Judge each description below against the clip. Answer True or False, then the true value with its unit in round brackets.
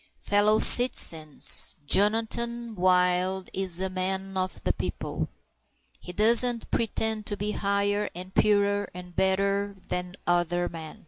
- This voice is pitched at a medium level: False (195 Hz)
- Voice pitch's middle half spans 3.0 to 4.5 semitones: False (2.6 semitones)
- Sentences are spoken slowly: True (125 wpm)